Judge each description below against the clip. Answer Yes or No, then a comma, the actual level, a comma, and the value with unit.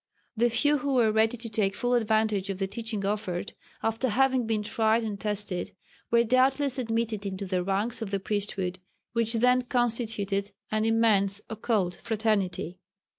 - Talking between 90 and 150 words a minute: No, average, 160 wpm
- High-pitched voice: Yes, high, 220 Hz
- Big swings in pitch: No, average, 2.8 semitones